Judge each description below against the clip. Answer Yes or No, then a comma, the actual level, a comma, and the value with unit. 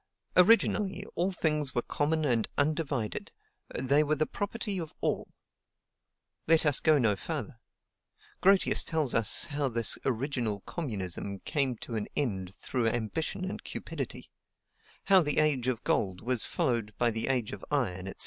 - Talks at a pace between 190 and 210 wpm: No, average, 150 wpm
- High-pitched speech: No, low, 135 Hz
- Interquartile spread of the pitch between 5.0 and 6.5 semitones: Yes, wide, 5.6 semitones